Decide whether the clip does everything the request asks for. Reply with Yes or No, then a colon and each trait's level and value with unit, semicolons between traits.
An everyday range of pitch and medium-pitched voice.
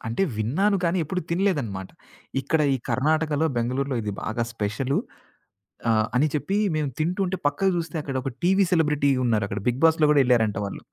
No: wide, 5.8 semitones; medium, 145 Hz